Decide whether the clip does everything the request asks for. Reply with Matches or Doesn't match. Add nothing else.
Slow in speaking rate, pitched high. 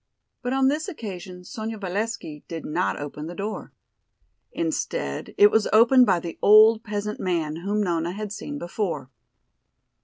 Doesn't match